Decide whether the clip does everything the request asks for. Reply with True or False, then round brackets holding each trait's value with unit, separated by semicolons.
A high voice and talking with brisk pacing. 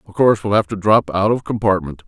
False (100 Hz; 260 wpm)